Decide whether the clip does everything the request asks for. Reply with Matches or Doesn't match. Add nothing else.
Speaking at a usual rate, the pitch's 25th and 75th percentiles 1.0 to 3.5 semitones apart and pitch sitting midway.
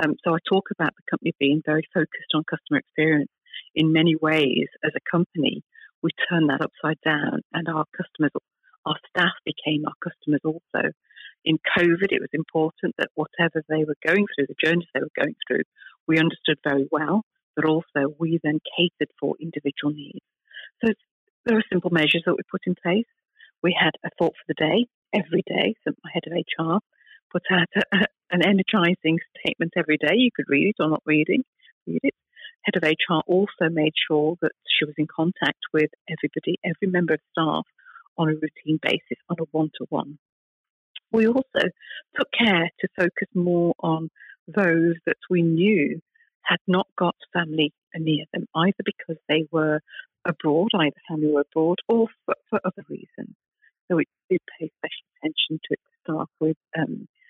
Matches